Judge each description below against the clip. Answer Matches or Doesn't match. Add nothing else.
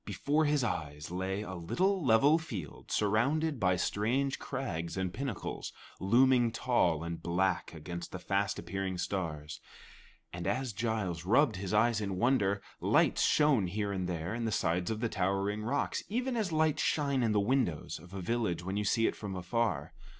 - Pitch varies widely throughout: Matches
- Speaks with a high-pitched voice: Doesn't match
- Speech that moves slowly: Doesn't match